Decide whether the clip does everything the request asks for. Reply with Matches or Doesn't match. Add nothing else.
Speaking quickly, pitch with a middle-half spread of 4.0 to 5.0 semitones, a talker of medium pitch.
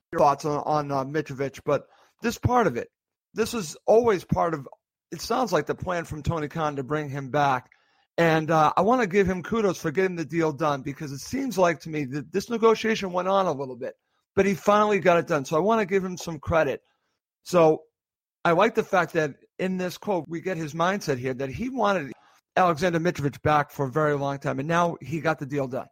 Matches